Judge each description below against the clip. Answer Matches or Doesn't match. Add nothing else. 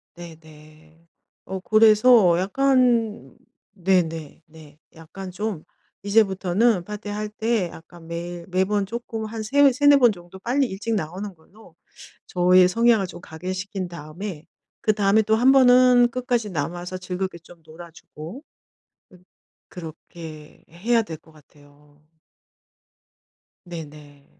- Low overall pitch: Doesn't match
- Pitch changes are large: Doesn't match